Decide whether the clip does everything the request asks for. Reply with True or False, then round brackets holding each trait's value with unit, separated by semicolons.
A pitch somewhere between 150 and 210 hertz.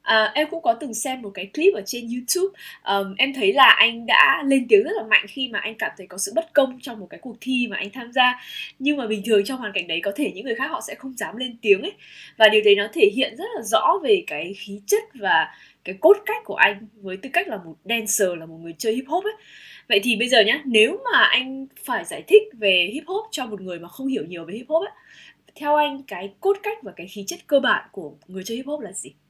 False (245 Hz)